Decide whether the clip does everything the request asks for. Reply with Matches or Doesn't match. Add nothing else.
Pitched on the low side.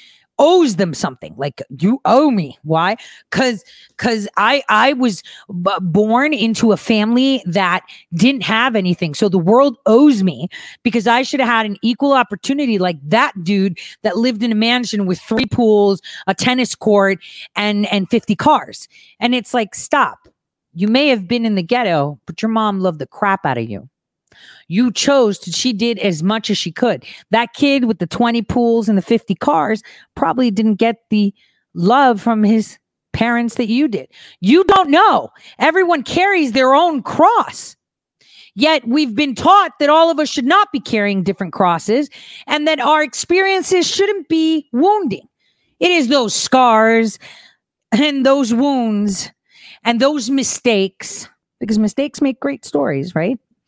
Doesn't match